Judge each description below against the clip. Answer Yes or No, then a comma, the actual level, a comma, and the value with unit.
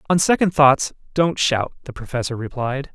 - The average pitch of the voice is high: No, medium, 140 Hz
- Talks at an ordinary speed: Yes, average, 165 wpm